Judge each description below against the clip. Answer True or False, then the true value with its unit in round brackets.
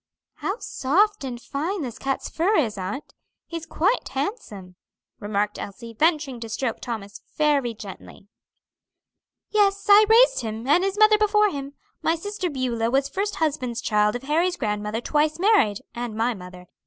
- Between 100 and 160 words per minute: True (155 wpm)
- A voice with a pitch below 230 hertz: False (275 Hz)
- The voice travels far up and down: True (8.6 semitones)